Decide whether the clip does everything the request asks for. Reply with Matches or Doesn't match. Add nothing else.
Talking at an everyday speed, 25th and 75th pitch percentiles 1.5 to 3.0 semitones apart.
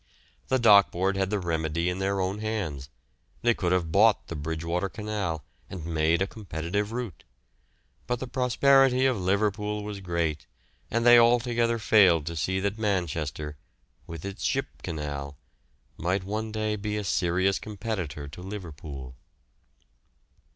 Doesn't match